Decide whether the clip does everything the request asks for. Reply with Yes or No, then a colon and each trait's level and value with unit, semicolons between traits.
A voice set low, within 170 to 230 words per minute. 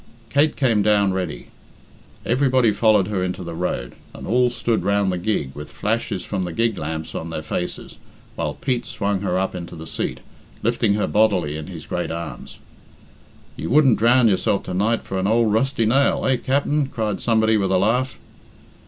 Yes: low, 105 Hz; average, 185 wpm